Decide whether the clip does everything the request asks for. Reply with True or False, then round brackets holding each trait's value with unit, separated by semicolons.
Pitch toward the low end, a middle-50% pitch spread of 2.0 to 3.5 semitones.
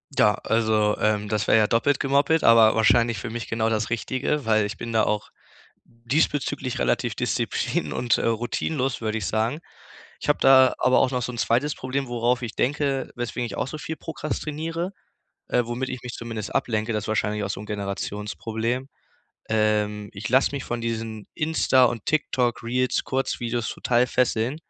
True (120 Hz; 3.1 semitones)